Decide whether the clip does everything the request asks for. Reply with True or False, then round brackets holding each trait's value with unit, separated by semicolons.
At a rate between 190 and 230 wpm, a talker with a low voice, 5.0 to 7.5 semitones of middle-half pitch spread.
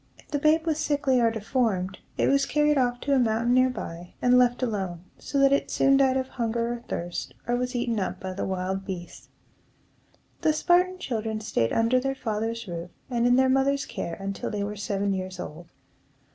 False (200 wpm; 235 Hz; 5.3 semitones)